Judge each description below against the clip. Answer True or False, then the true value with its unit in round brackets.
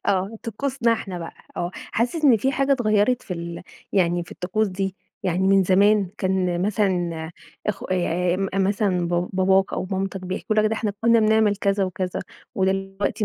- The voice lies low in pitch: False (195 Hz)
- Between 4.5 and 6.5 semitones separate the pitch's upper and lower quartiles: False (2.9 semitones)